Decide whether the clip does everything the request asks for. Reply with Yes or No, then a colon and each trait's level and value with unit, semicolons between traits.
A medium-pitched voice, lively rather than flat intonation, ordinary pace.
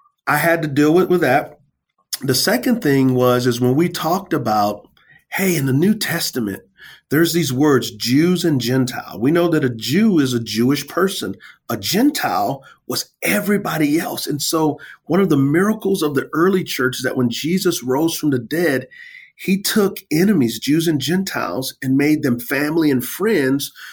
Yes: medium, 155 Hz; wide, 5.8 semitones; average, 180 wpm